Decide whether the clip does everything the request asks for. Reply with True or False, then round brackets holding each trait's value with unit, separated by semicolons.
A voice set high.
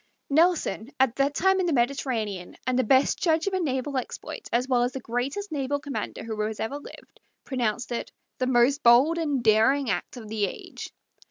True (260 Hz)